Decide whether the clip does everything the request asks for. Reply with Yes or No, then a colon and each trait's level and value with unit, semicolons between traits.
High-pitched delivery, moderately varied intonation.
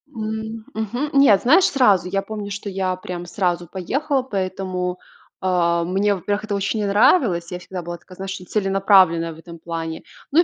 Yes: high, 195 Hz; average, 3.2 semitones